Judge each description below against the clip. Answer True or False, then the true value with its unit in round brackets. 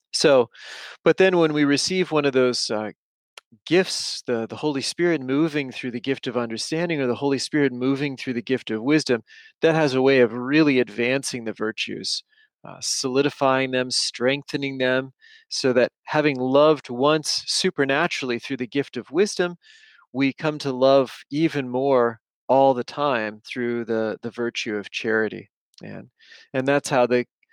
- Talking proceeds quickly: False (165 wpm)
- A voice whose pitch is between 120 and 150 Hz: True (135 Hz)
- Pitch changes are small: False (3.6 semitones)